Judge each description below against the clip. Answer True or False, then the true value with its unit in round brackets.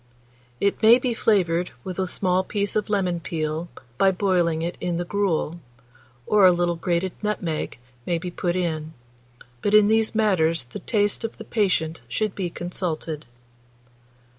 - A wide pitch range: False (3.5 semitones)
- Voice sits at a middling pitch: True (180 Hz)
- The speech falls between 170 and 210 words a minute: False (160 wpm)